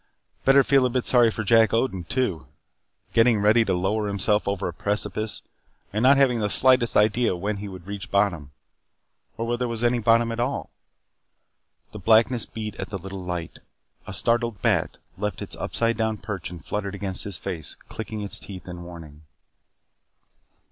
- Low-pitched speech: Yes, low, 105 Hz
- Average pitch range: Yes, average, 3.3 semitones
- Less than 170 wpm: No, average, 175 wpm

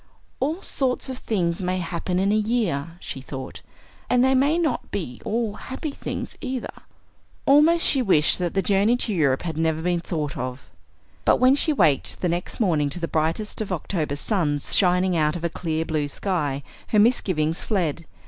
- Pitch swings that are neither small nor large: No, wide, 6.6 semitones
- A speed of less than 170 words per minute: No, average, 185 wpm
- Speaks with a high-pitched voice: No, medium, 180 Hz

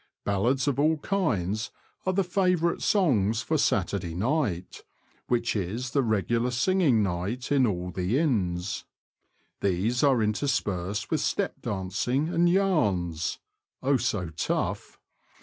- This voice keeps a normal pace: No, slow, 130 wpm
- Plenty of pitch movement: Yes, wide, 7.2 semitones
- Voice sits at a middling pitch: No, low, 120 Hz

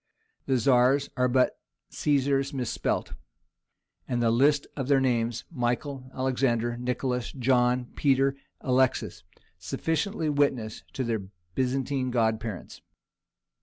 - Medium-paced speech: No, slow, 95 wpm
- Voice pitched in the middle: No, low, 130 Hz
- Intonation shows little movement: Yes, narrow, 2.3 semitones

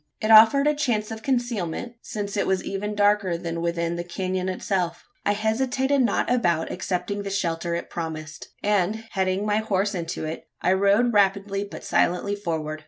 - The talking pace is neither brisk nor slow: Yes, average, 170 wpm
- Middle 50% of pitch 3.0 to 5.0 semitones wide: Yes, average, 3.7 semitones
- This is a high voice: Yes, high, 200 Hz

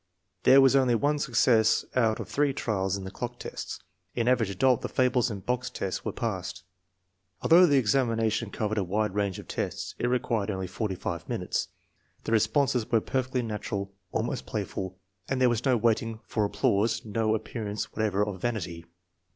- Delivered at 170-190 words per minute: Yes, average, 175 wpm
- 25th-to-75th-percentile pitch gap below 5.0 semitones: Yes, average, 3.6 semitones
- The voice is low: Yes, low, 110 Hz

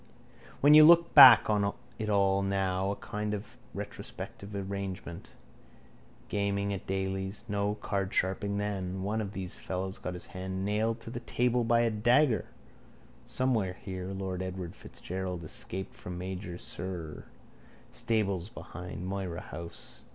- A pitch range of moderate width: No, narrow, 2.3 semitones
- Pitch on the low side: Yes, low, 100 Hz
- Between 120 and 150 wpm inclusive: Yes, average, 140 wpm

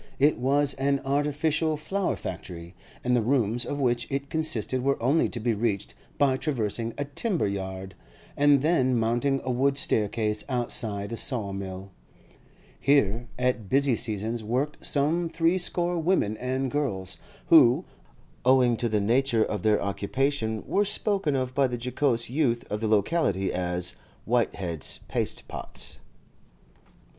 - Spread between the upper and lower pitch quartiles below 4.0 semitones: No, average, 4.8 semitones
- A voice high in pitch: No, low, 125 Hz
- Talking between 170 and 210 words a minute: No, average, 140 wpm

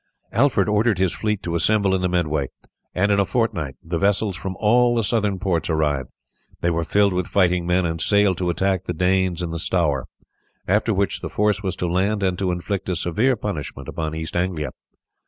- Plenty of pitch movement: No, average, 3.2 semitones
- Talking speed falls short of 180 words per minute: No, fast, 205 wpm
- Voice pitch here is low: Yes, very low, 95 Hz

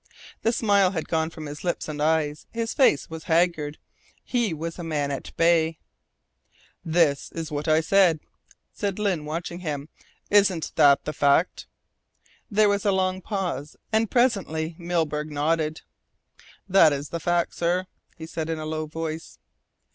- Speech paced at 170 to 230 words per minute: No, average, 155 wpm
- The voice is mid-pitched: Yes, medium, 165 Hz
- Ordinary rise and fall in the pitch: Yes, average, 3.3 semitones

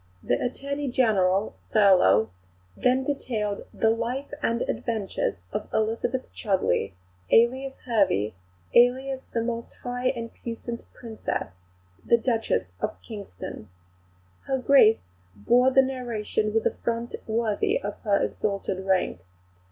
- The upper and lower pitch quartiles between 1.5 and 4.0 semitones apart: Yes, average, 3.7 semitones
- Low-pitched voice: No, high, 230 Hz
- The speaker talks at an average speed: No, slow, 120 wpm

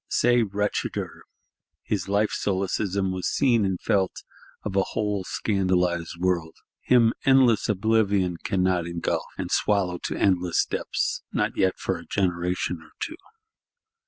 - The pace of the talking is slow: Yes, slow, 130 wpm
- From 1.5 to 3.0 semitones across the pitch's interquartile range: Yes, narrow, 2.6 semitones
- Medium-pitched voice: No, very low, 95 Hz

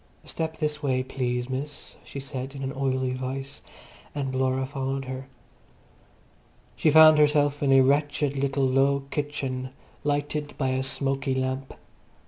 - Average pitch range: No, narrow, 1.8 semitones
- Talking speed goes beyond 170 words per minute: No, average, 140 wpm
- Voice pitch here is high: No, low, 135 Hz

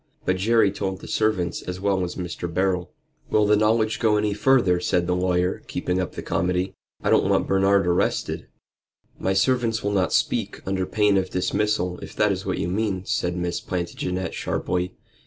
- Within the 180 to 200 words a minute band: Yes, average, 185 wpm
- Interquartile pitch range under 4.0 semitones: Yes, average, 2.7 semitones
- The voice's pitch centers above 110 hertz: No, very low, 95 Hz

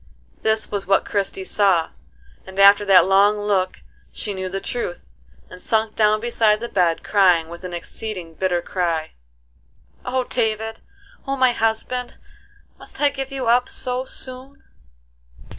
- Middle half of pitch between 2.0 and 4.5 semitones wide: Yes, average, 4.1 semitones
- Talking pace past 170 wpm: No, average, 145 wpm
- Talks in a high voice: Yes, high, 210 Hz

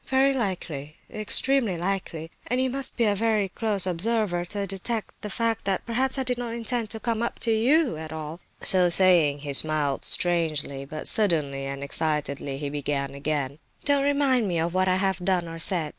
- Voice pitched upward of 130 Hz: Yes, medium, 185 Hz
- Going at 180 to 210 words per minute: Yes, average, 190 wpm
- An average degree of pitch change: No, wide, 6.7 semitones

